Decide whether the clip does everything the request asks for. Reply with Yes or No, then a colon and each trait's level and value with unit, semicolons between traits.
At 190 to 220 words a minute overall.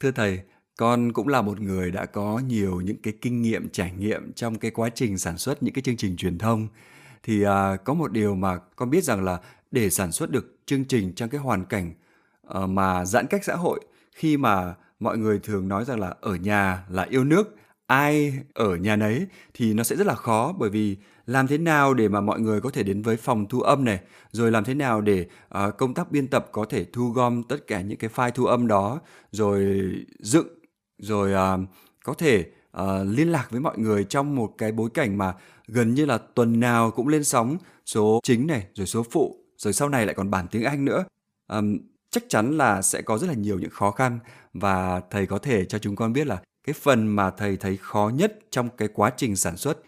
No: average, 230 wpm